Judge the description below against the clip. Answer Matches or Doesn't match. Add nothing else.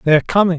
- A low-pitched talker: Doesn't match